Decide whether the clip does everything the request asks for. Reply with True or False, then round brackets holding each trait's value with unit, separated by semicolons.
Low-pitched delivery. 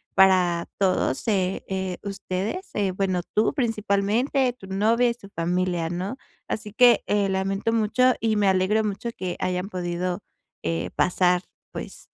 False (195 Hz)